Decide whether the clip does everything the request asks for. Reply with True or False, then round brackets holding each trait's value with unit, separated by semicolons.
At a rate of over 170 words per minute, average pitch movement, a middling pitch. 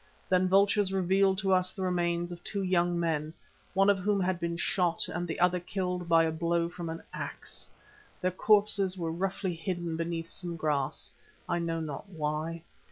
False (180 wpm; 2.1 semitones; 175 Hz)